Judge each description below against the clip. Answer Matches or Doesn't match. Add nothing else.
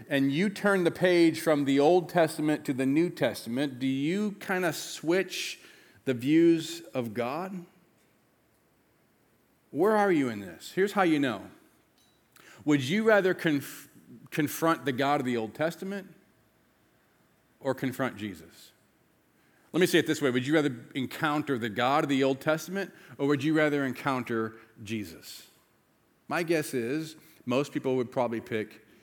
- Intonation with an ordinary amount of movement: Matches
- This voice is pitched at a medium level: Matches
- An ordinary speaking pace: Matches